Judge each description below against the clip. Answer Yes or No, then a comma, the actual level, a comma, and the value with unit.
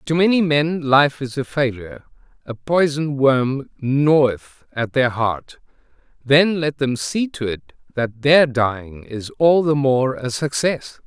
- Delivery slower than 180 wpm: Yes, average, 155 wpm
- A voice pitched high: No, low, 135 Hz